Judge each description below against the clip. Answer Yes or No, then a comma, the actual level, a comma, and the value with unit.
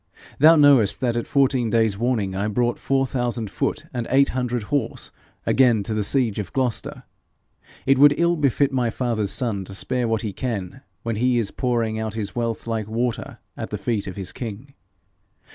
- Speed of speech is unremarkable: Yes, average, 190 wpm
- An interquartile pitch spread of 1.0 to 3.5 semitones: Yes, average, 3.2 semitones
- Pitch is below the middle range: Yes, low, 120 Hz